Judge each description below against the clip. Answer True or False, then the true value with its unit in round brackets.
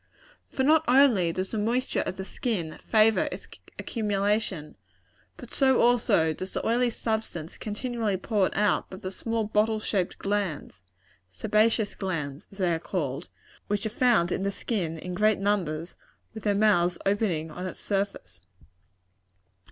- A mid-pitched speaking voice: False (205 Hz)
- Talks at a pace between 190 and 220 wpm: False (150 wpm)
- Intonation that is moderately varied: True (3.8 semitones)